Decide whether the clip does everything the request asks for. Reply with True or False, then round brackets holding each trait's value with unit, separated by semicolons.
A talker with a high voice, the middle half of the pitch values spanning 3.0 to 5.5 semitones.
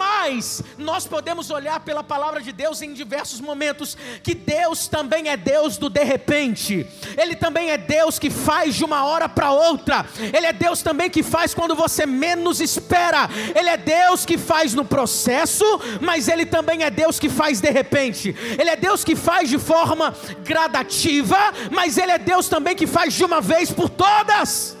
False (315 Hz; 2.5 semitones)